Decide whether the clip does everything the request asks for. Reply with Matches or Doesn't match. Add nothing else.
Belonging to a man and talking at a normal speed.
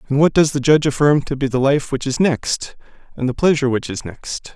Doesn't match